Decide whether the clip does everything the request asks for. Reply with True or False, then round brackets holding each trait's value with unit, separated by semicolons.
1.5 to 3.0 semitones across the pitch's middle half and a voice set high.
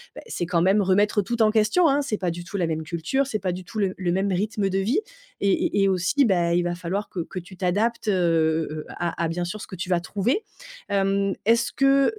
False (3.4 semitones; 195 Hz)